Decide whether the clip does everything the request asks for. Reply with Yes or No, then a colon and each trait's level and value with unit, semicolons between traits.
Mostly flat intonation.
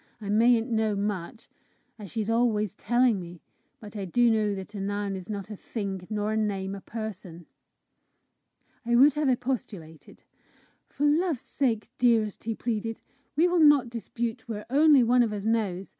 No: average, 3.2 semitones